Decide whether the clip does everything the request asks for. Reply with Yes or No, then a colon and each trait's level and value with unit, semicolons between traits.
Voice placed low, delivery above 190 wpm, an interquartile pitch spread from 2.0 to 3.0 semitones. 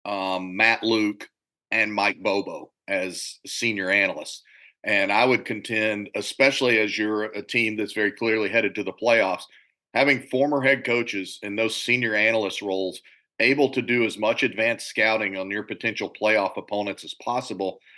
No: low, 110 Hz; average, 160 wpm; narrow, 2.4 semitones